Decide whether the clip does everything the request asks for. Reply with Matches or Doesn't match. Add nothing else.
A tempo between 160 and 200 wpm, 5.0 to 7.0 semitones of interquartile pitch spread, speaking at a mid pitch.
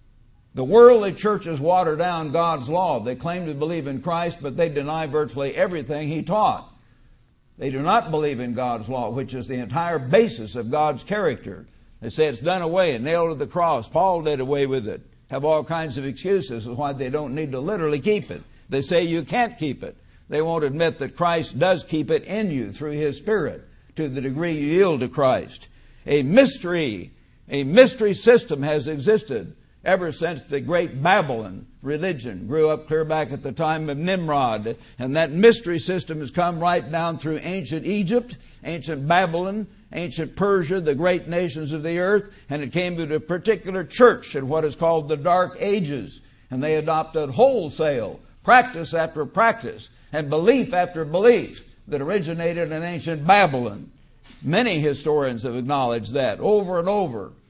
Doesn't match